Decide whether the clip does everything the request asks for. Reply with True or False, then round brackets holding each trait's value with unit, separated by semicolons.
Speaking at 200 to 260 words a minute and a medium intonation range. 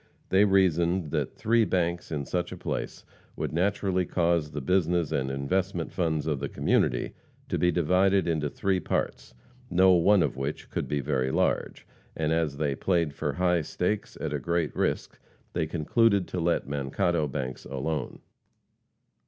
False (160 wpm; 3.7 semitones)